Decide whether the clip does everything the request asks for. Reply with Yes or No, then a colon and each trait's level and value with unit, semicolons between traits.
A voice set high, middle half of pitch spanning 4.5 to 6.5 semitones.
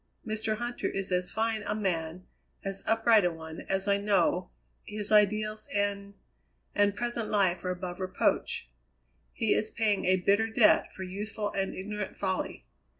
No: high, 200 Hz; narrow, 2.4 semitones